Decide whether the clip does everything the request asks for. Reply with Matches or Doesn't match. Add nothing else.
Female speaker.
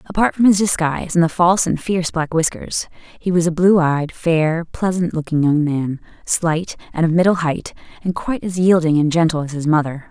Matches